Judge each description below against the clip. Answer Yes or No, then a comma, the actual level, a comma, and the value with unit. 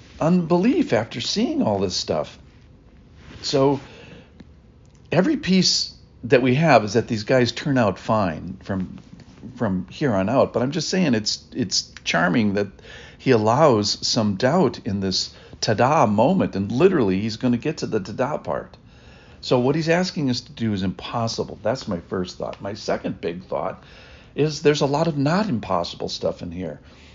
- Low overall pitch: Yes, low, 125 Hz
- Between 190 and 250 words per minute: No, average, 170 wpm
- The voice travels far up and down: Yes, wide, 6.3 semitones